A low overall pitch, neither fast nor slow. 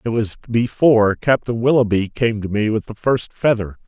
Yes: low, 115 Hz; average, 185 wpm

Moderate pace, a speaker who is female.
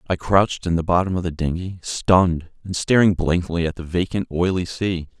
No: average, 195 wpm; male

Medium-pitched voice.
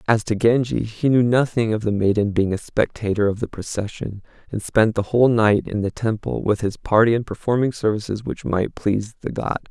No: low, 110 Hz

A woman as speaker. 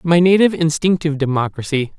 No: male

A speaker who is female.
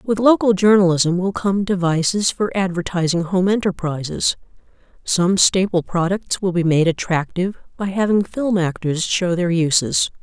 Yes: female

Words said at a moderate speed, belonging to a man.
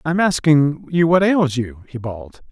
Yes: average, 190 wpm; male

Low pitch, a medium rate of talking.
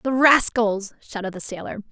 No: high, 220 Hz; average, 155 wpm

